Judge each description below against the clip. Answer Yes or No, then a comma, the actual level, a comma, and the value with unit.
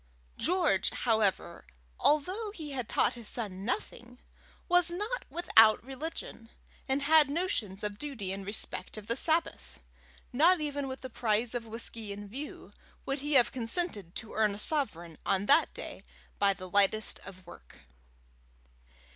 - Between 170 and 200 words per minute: No, average, 150 wpm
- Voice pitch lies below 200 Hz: No, high, 235 Hz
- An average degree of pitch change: No, wide, 6.5 semitones